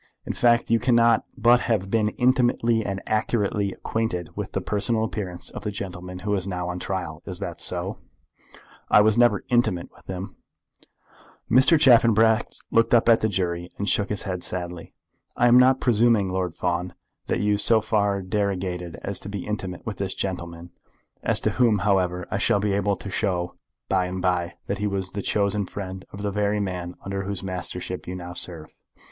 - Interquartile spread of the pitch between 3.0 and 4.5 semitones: Yes, average, 3.3 semitones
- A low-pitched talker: Yes, low, 100 Hz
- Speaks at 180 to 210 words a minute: Yes, average, 190 wpm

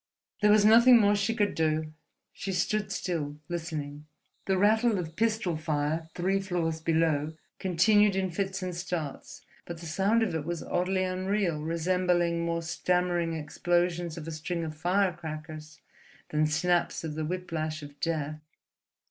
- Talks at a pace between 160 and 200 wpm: No, average, 150 wpm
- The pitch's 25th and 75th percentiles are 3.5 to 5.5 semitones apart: No, average, 3.1 semitones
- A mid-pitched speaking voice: Yes, medium, 170 Hz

